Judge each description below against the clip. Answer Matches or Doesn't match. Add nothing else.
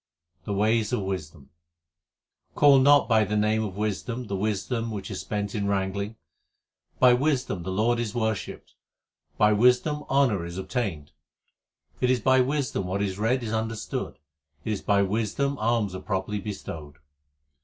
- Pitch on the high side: Doesn't match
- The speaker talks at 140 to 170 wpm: Matches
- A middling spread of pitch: Matches